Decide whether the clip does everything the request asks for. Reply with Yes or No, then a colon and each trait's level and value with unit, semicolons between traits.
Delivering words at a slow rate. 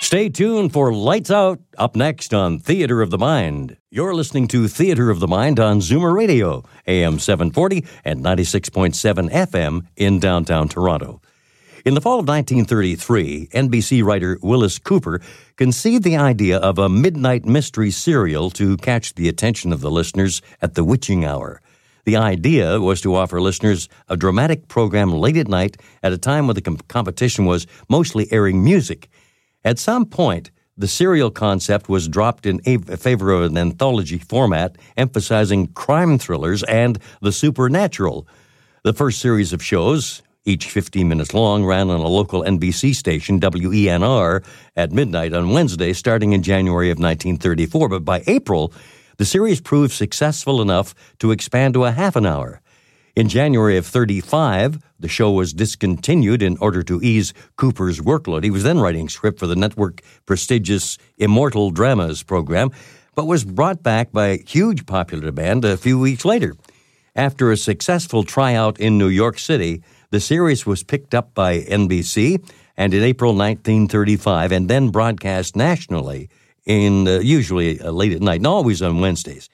No: average, 160 wpm